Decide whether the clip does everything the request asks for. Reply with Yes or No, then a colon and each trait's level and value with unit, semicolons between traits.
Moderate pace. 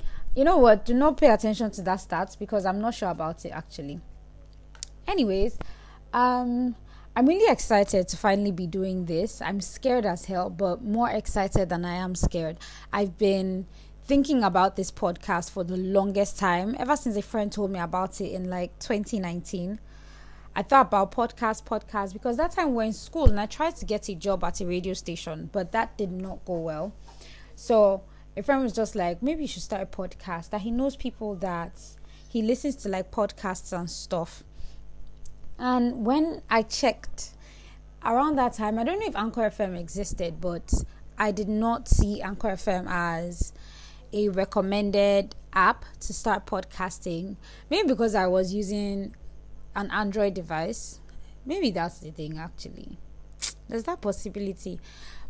Yes: average, 170 wpm